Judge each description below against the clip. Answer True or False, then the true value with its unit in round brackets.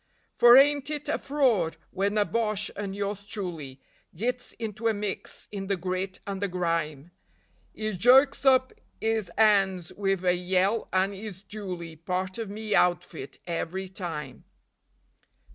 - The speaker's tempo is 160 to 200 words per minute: False (145 wpm)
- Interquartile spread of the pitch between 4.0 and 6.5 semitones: False (3.4 semitones)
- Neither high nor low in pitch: False (195 Hz)